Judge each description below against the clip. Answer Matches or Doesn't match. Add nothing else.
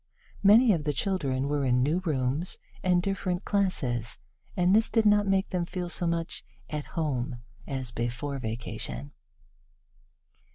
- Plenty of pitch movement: Matches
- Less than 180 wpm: Matches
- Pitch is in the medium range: Matches